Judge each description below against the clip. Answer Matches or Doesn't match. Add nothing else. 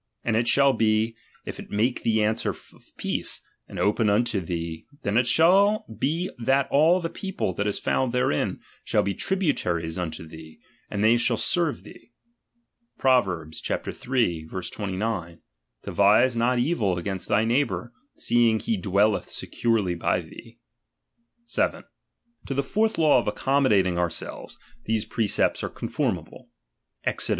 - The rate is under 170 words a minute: Matches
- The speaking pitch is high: Doesn't match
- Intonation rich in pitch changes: Matches